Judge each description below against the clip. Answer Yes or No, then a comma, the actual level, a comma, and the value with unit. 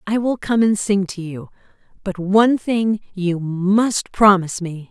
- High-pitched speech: Yes, high, 200 Hz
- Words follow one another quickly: No, average, 160 wpm